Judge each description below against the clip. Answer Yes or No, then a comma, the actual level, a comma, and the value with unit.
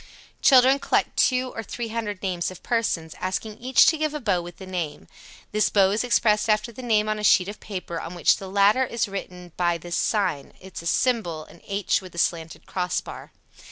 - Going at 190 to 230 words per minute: Yes, average, 195 wpm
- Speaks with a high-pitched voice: Yes, high, 200 Hz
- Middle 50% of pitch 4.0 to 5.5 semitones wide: Yes, average, 4.5 semitones